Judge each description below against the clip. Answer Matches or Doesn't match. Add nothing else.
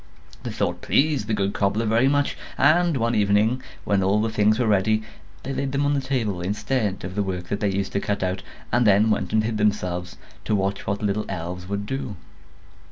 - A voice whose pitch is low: Matches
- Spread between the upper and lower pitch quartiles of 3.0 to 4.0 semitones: Matches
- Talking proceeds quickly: Matches